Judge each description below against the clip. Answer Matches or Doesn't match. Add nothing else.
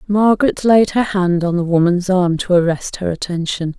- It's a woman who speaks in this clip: Matches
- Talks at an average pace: Matches